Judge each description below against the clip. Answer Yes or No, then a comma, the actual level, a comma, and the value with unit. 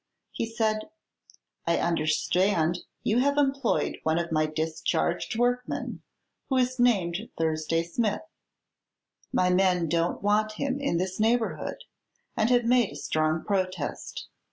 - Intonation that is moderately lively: No, wide, 6.1 semitones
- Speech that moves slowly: Yes, slow, 130 wpm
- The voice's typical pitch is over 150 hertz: Yes, high, 190 Hz